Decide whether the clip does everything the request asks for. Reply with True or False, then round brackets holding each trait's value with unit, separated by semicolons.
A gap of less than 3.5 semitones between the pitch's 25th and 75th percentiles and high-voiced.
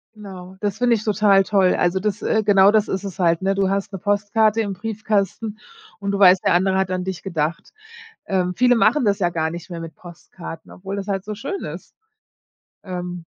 True (2.5 semitones; 195 Hz)